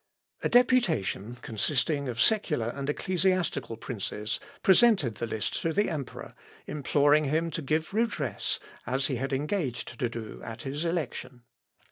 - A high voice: No, medium, 140 Hz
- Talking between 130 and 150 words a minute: Yes, average, 140 wpm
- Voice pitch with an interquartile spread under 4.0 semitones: No, wide, 5.6 semitones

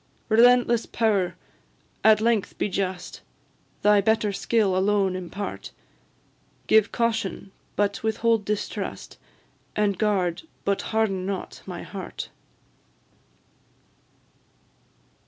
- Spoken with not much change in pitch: Yes, narrow, 2.3 semitones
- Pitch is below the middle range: No, high, 205 Hz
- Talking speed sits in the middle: No, slow, 90 wpm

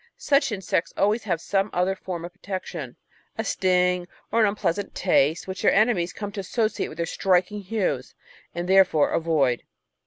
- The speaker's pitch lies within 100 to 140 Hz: No, high, 190 Hz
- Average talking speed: Yes, average, 165 wpm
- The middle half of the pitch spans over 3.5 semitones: No, average, 2.9 semitones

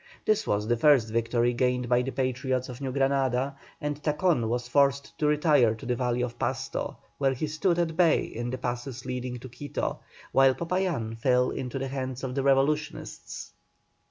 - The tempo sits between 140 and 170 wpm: No, average, 185 wpm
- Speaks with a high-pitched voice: No, low, 130 Hz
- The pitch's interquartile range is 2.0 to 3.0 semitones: Yes, average, 2.7 semitones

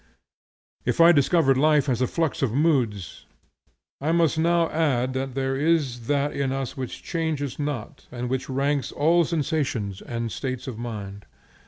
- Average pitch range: Yes, average, 4.0 semitones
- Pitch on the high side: No, low, 135 Hz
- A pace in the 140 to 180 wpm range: Yes, average, 165 wpm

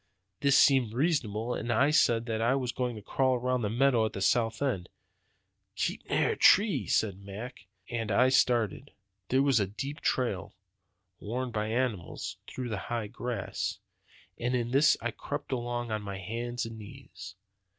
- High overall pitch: No, low, 120 Hz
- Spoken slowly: No, average, 170 wpm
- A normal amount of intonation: Yes, average, 3.0 semitones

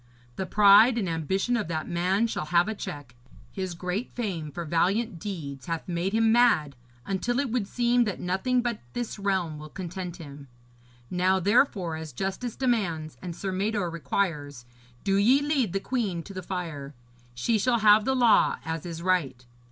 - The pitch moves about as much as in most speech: Yes, average, 5.0 semitones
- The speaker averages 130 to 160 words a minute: No, average, 175 wpm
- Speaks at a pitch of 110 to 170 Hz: No, high, 190 Hz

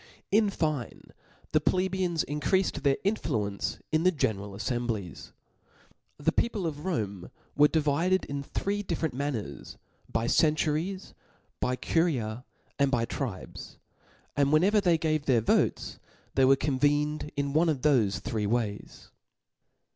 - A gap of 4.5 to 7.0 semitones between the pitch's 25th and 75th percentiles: Yes, wide, 5.5 semitones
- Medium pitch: Yes, medium, 145 Hz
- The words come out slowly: Yes, slow, 125 wpm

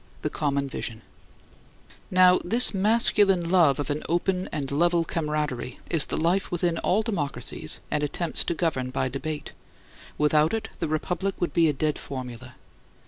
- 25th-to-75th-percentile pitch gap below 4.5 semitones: Yes, average, 4.1 semitones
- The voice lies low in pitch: No, medium, 160 Hz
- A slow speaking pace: No, average, 155 wpm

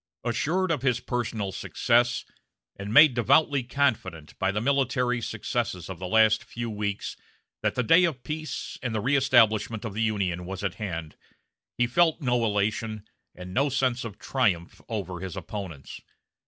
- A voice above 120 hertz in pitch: No, low, 115 Hz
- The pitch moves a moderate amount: Yes, average, 4.1 semitones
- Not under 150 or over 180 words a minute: Yes, average, 160 wpm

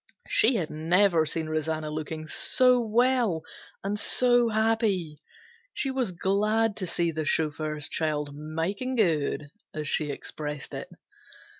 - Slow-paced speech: Yes, slow, 130 wpm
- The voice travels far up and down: Yes, wide, 6.2 semitones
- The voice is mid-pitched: Yes, medium, 170 Hz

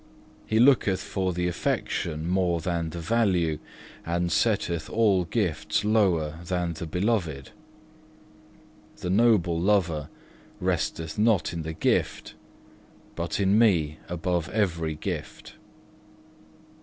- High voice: No, very low, 90 Hz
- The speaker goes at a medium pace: No, slow, 110 wpm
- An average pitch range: Yes, average, 3.7 semitones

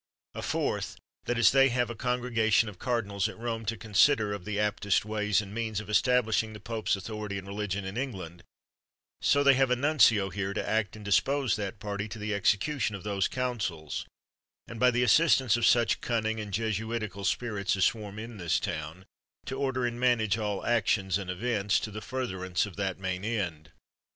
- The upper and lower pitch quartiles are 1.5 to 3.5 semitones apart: Yes, average, 3.2 semitones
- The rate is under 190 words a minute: No, average, 195 wpm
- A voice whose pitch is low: Yes, low, 110 Hz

